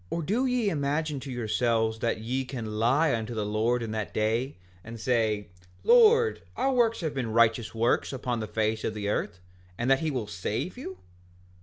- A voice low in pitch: Yes, low, 115 Hz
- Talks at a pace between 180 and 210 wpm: Yes, average, 185 wpm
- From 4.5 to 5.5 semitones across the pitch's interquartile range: Yes, average, 5.1 semitones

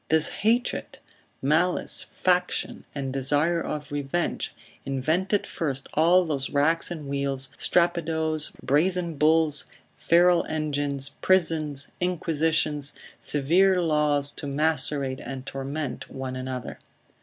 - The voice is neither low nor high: Yes, medium, 150 Hz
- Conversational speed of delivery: No, slow, 105 wpm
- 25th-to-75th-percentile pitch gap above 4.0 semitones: No, average, 3.3 semitones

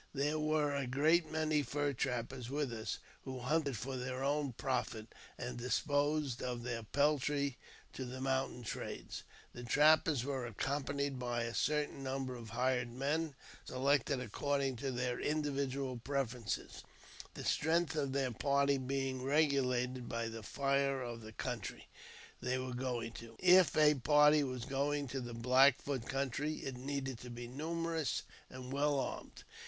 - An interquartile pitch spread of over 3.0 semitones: No, narrow, 2.6 semitones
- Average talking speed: Yes, average, 155 wpm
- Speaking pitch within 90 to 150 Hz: Yes, low, 135 Hz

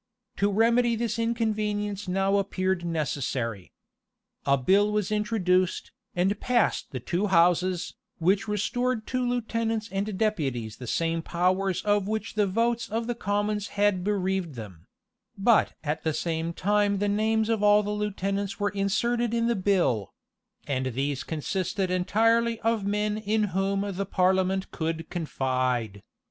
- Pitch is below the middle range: No, high, 200 Hz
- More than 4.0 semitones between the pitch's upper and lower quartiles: No, average, 3.6 semitones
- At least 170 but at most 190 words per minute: No, average, 145 wpm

